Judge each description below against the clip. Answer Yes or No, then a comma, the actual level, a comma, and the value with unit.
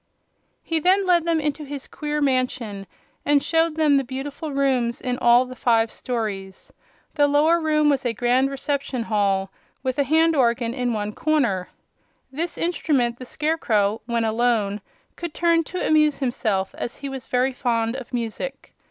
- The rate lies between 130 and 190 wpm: Yes, average, 165 wpm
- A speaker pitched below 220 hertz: No, very high, 260 Hz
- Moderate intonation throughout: Yes, average, 4.4 semitones